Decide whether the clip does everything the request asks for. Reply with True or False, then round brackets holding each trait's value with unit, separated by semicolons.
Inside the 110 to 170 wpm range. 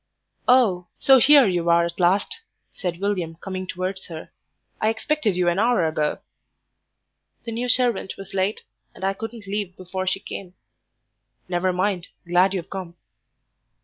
True (150 wpm)